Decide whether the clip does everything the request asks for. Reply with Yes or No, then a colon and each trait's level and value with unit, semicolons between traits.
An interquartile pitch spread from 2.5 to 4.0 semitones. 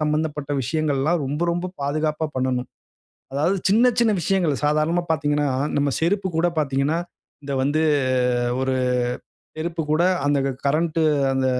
Yes: average, 2.9 semitones